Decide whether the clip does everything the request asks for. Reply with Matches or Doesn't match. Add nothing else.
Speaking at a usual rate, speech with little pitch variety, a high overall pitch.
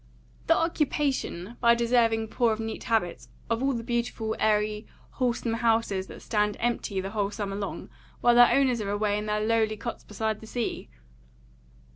Matches